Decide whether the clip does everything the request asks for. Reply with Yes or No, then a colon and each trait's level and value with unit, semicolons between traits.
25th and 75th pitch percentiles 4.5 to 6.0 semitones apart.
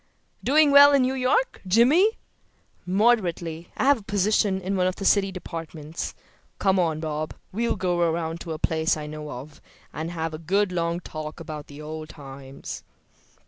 Yes: average, 4.8 semitones